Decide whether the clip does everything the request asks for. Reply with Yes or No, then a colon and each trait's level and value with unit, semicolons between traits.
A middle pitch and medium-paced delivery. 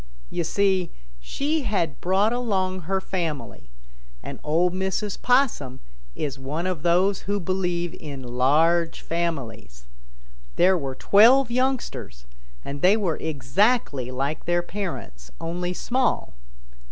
No: medium, 175 Hz; slow, 120 wpm